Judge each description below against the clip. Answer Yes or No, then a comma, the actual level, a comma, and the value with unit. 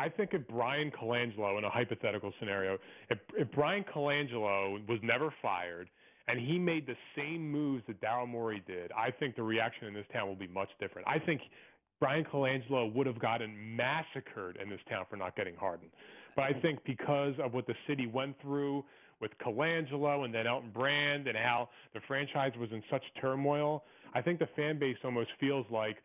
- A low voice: Yes, low, 130 Hz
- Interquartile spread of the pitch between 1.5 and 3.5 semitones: No, average, 4.3 semitones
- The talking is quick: No, average, 195 wpm